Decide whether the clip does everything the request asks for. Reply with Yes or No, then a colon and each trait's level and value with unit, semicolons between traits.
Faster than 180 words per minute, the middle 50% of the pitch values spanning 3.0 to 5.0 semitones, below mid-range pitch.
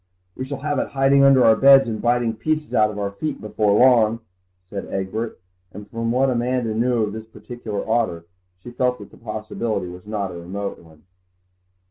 Yes: average, 190 wpm; average, 3.5 semitones; low, 115 Hz